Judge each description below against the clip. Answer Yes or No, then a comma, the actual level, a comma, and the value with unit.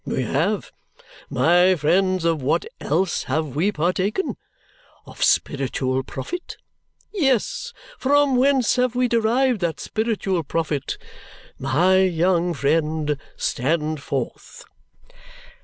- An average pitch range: No, wide, 7.1 semitones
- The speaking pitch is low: No, medium, 180 Hz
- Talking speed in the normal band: No, slow, 105 wpm